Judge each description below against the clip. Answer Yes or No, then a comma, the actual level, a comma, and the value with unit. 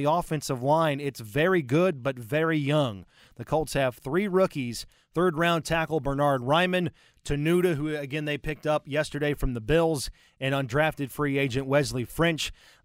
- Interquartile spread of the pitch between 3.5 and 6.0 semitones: No, average, 2.9 semitones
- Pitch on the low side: No, medium, 150 Hz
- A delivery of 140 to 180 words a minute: Yes, average, 165 wpm